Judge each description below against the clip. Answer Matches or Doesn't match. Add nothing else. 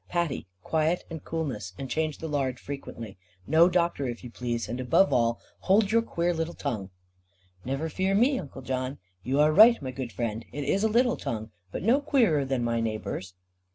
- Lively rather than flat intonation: Matches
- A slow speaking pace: Doesn't match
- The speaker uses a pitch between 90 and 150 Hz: Matches